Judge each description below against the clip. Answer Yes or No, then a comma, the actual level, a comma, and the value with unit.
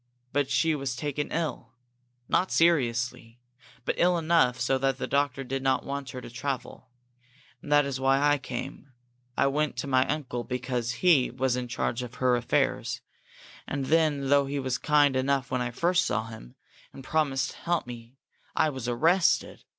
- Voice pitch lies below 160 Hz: Yes, low, 135 Hz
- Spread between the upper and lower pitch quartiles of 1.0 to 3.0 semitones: Yes, average, 2.7 semitones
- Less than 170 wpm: No, average, 180 wpm